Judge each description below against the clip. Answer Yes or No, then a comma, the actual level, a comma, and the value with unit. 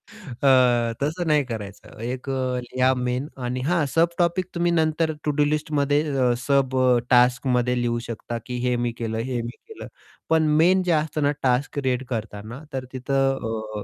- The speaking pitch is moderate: No, low, 130 Hz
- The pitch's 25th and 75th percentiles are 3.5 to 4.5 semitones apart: Yes, average, 3.8 semitones